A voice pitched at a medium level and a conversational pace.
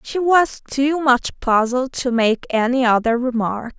No: very high, 250 Hz; average, 160 wpm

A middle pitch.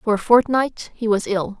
No: high, 220 Hz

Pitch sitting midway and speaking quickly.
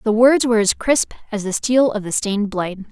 No: high, 220 Hz; fast, 245 wpm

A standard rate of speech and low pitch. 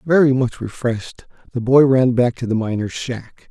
Yes: average, 190 wpm; low, 125 Hz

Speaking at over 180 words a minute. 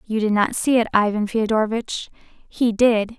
No: average, 170 wpm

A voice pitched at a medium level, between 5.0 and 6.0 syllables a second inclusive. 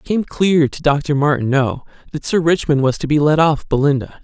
Yes: medium, 150 Hz; 5.6 syllables/s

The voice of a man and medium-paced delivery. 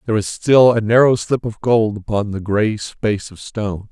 No: male; fast, 215 wpm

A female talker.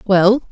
Yes: female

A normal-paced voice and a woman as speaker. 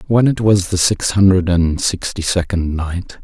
No: average, 185 wpm; male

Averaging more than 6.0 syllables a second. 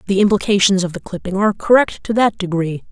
Yes: 6.3 syllables/s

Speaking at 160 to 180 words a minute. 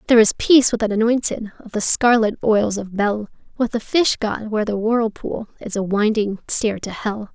No: fast, 205 wpm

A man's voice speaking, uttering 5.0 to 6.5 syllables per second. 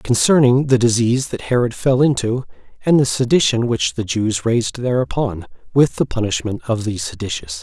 Yes: male; 5.3 syllables/s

